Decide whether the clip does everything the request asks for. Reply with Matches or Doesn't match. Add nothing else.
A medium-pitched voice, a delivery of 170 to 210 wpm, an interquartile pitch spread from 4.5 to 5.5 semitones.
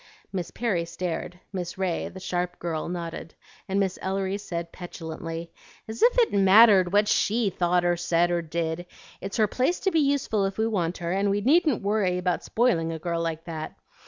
Doesn't match